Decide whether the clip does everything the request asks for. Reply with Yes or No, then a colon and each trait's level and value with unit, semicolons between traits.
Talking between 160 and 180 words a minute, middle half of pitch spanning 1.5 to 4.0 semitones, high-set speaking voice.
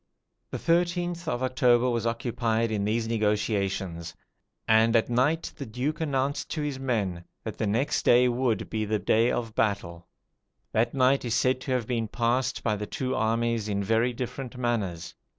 No: average, 175 wpm; average, 3.0 semitones; low, 115 Hz